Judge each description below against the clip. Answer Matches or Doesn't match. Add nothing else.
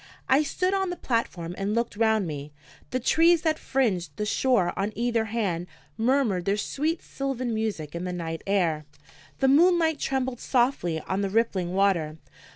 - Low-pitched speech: Doesn't match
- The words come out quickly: Doesn't match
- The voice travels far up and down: Matches